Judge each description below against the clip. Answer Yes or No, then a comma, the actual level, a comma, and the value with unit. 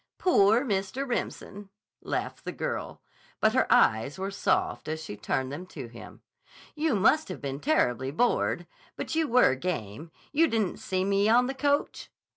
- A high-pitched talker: Yes, high, 195 Hz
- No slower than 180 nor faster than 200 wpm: No, average, 165 wpm